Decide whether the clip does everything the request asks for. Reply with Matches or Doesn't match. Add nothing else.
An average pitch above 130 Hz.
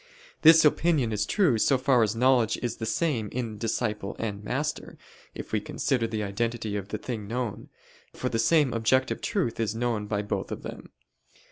Doesn't match